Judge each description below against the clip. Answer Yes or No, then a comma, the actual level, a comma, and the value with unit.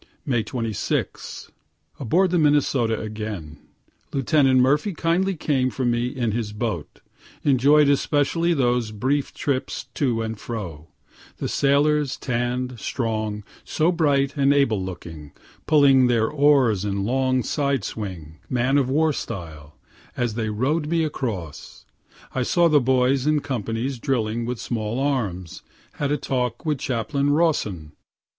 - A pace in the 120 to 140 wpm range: Yes, slow, 135 wpm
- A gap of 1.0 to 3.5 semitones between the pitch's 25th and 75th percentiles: No, average, 4.6 semitones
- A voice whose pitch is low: Yes, low, 125 Hz